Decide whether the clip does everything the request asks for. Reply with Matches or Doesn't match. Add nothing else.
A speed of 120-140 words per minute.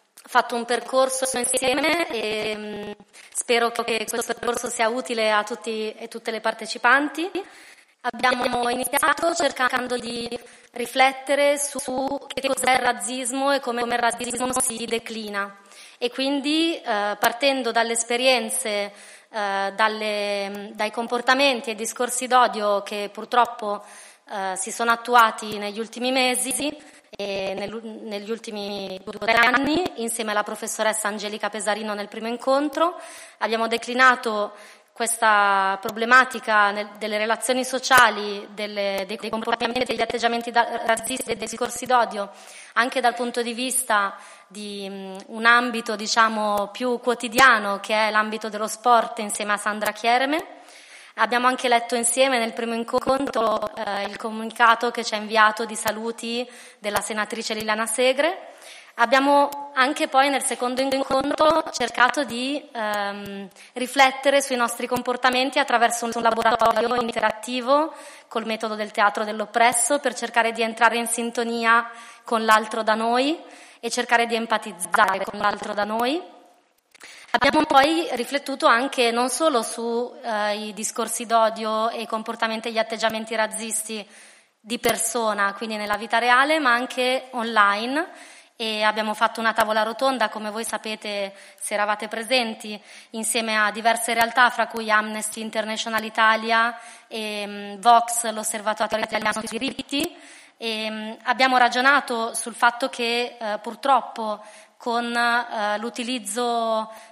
Matches